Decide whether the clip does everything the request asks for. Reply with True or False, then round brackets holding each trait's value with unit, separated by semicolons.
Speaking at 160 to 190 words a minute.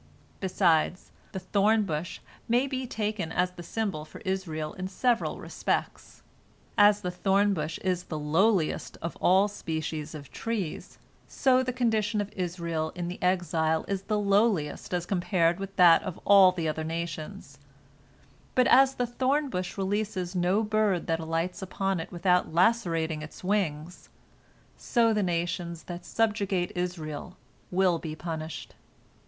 False (150 wpm)